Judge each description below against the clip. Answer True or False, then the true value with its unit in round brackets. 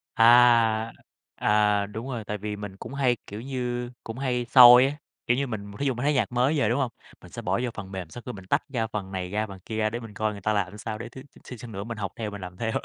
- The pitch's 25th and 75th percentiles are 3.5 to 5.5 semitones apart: False (3.1 semitones)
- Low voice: True (110 Hz)